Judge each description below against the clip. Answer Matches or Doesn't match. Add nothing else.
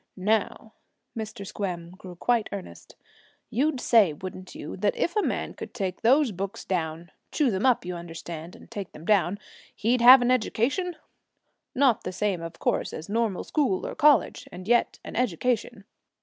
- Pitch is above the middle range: Matches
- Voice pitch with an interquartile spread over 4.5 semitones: Matches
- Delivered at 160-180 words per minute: Matches